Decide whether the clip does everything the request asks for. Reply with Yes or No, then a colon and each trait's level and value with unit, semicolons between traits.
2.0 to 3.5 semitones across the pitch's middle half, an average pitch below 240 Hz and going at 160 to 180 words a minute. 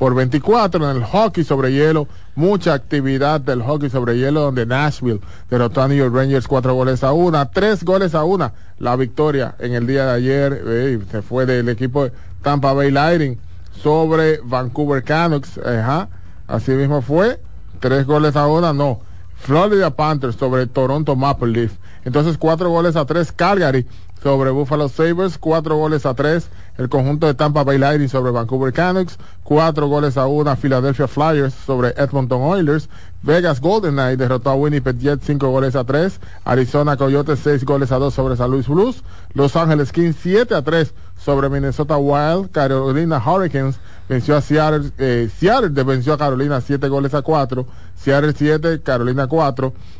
Yes: average, 2.8 semitones; medium, 140 Hz; average, 170 wpm